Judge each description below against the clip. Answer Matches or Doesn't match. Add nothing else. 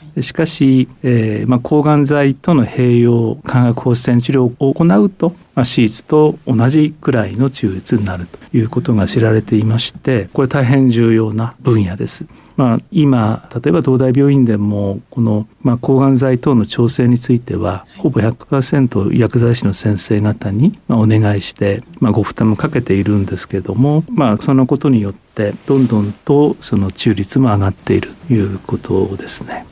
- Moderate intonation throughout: Matches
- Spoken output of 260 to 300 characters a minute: Doesn't match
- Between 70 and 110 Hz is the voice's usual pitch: Doesn't match